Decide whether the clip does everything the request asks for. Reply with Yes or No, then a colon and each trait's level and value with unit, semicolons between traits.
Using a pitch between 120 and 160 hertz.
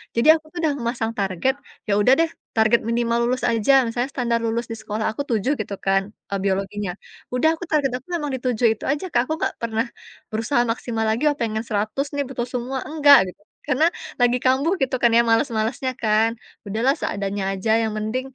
No: high, 235 Hz